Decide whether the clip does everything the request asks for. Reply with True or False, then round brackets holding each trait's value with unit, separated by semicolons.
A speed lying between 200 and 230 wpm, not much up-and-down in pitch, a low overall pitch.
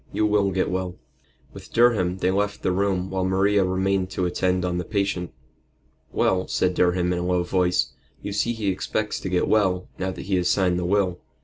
True (205 wpm; 1.7 semitones; 95 Hz)